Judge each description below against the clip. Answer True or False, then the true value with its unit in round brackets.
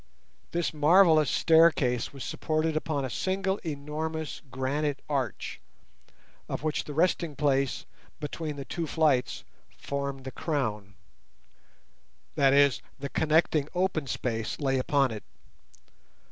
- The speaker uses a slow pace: True (120 wpm)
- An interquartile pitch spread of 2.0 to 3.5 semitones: True (2.9 semitones)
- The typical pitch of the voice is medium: True (145 Hz)